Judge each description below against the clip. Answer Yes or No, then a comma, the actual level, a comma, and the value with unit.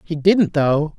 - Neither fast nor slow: Yes, average, 185 wpm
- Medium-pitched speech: Yes, medium, 160 Hz